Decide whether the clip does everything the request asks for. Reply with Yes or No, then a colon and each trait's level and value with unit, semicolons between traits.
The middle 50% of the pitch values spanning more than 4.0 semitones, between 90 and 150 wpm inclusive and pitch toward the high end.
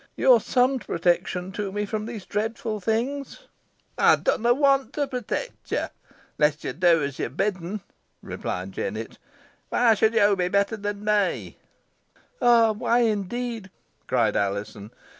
Yes: average, 4.8 semitones; average, 140 wpm; high, 210 Hz